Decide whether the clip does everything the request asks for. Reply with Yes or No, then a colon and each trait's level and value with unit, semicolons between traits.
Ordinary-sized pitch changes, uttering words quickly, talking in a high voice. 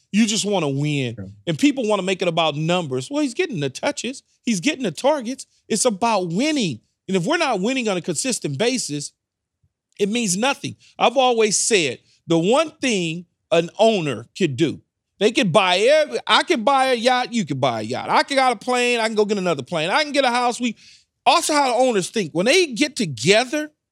No: wide, 7.2 semitones; fast, 220 wpm; high, 215 Hz